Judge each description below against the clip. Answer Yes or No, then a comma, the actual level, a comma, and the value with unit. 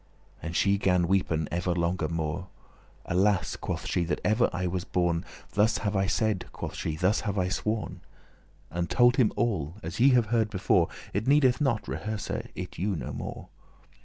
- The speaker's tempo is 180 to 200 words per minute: Yes, average, 185 wpm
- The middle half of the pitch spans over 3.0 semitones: Yes, average, 3.9 semitones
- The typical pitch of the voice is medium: No, very low, 95 Hz